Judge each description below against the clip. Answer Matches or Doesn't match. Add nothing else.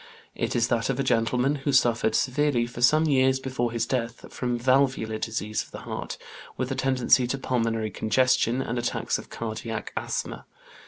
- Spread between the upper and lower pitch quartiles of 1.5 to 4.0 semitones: Matches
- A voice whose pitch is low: Matches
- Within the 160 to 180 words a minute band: Matches